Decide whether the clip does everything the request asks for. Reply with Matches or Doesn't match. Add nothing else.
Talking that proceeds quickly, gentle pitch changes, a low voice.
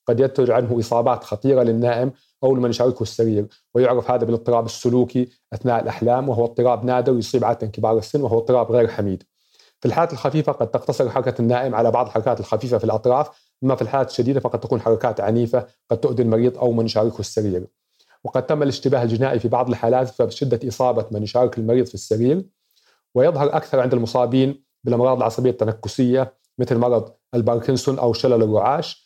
Matches